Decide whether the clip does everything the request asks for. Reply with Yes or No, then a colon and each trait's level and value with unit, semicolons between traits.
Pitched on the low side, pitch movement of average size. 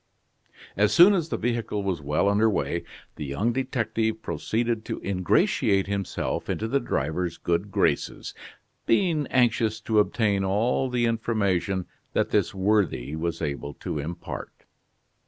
Yes: low, 105 Hz; average, 4.1 semitones